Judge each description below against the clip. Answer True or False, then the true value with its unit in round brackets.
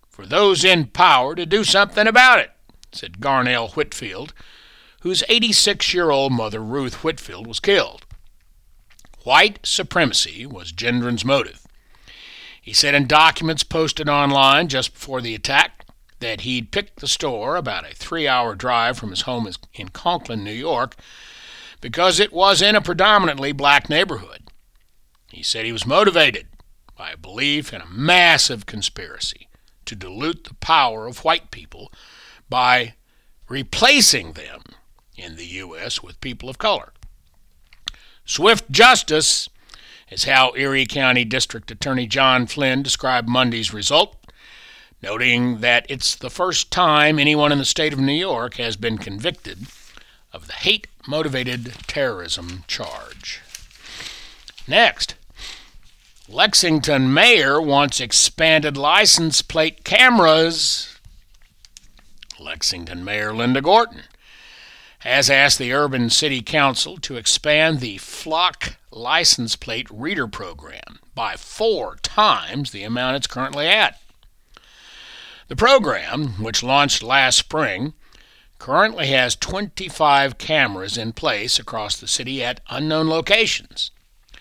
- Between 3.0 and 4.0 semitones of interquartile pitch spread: False (5.2 semitones)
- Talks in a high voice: False (135 Hz)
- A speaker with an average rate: False (125 wpm)